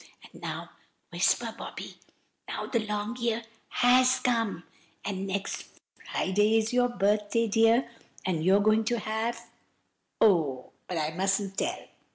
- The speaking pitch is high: Yes, high, 215 Hz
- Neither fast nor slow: No, slow, 130 wpm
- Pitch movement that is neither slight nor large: Yes, average, 3.1 semitones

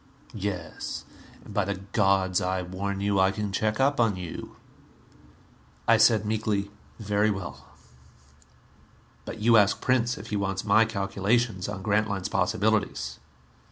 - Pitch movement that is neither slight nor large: No, narrow, 2.2 semitones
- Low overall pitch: Yes, low, 100 Hz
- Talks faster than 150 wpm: No, slow, 135 wpm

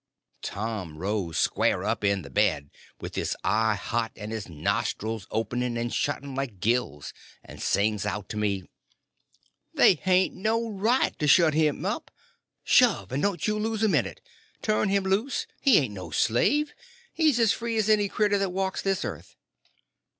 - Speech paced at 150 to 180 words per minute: Yes, average, 160 wpm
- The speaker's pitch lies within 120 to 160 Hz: Yes, low, 135 Hz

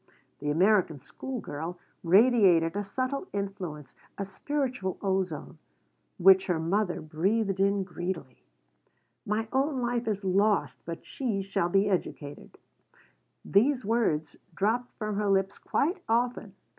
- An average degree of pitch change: Yes, average, 4.4 semitones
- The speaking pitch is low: No, high, 195 Hz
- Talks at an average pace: No, slow, 125 wpm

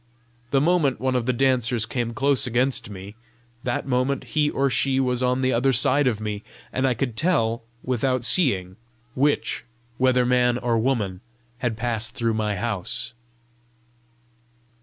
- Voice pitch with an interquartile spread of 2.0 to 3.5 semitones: Yes, narrow, 2.6 semitones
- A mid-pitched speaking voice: No, low, 125 Hz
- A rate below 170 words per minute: Yes, average, 155 wpm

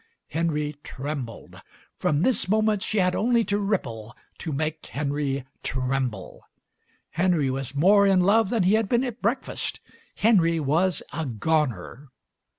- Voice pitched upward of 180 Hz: No, medium, 160 Hz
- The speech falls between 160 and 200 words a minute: No, average, 140 wpm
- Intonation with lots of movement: Yes, wide, 6.6 semitones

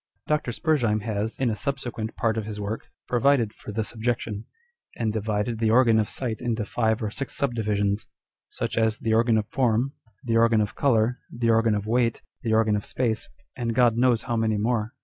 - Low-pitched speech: Yes, low, 115 Hz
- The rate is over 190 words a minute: Yes, average, 200 wpm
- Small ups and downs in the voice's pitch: Yes, narrow, 1.8 semitones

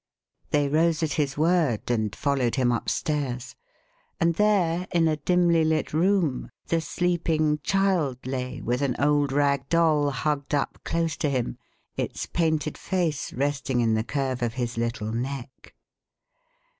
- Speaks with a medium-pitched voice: Yes, medium, 145 Hz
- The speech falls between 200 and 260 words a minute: No, average, 145 wpm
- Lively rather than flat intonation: No, average, 4.2 semitones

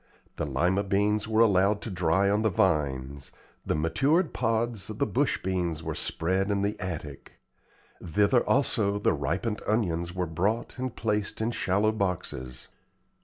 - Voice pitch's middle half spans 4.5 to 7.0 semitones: No, average, 4.1 semitones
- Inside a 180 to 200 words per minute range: No, average, 155 wpm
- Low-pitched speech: Yes, low, 100 Hz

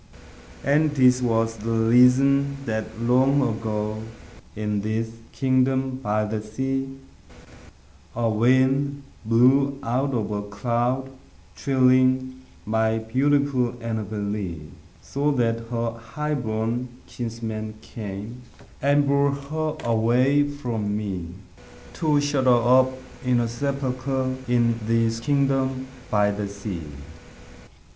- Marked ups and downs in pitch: No, average, 3.2 semitones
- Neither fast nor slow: No, slow, 110 wpm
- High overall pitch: No, low, 120 Hz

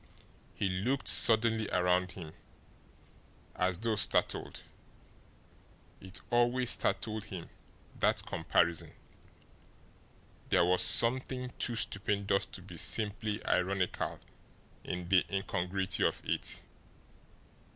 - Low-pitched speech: Yes, low, 100 Hz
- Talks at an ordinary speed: No, slow, 95 wpm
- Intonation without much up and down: No, average, 3.8 semitones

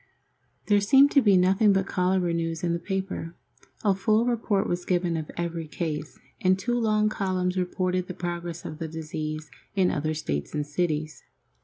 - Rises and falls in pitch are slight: No, average, 3.1 semitones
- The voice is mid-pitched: Yes, medium, 180 Hz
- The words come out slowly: No, average, 175 wpm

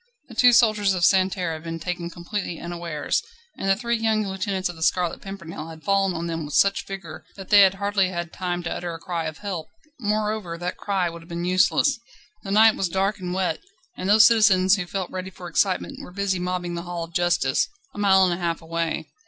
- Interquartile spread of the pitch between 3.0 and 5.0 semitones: No, narrow, 2.6 semitones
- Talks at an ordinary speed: No, fast, 225 wpm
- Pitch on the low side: No, medium, 185 Hz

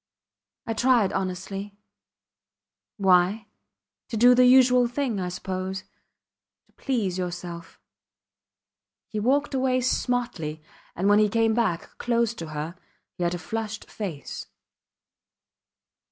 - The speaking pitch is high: Yes, high, 210 Hz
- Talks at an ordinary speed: No, slow, 115 wpm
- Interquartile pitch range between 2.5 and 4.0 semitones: No, average, 5.1 semitones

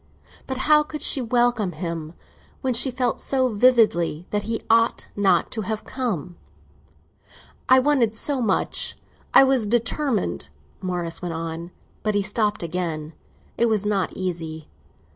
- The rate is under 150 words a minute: Yes, average, 140 wpm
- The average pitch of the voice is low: No, high, 215 Hz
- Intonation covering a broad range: Yes, wide, 6.0 semitones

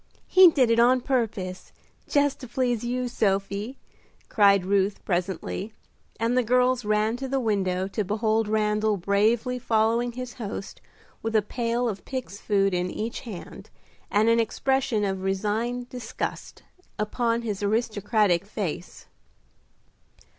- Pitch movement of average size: Yes, average, 3.3 semitones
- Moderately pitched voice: No, high, 220 Hz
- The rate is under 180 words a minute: Yes, slow, 135 wpm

